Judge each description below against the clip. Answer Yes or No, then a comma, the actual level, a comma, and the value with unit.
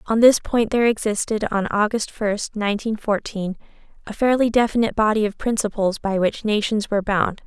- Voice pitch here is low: No, high, 215 Hz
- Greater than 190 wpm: No, average, 170 wpm